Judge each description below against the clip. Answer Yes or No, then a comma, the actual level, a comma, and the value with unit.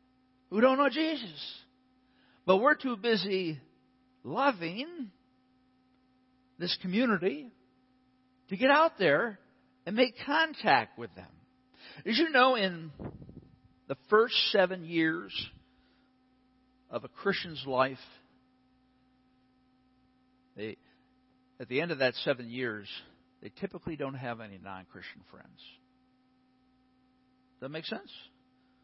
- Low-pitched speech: No, medium, 185 Hz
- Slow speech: Yes, slow, 105 wpm